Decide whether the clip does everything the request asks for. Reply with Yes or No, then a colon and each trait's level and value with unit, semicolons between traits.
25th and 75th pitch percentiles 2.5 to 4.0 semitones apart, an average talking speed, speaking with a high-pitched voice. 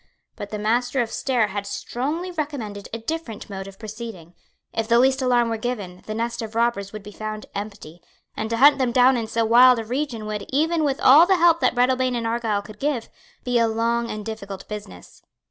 No: average, 3.2 semitones; fast, 215 wpm; high, 230 Hz